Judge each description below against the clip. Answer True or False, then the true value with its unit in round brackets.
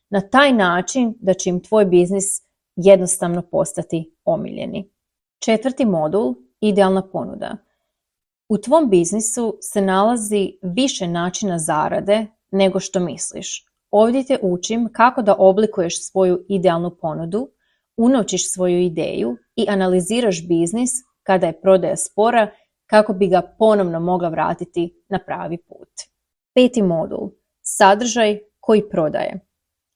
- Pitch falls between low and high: False (195 Hz)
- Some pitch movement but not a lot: True (3.4 semitones)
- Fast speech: False (120 wpm)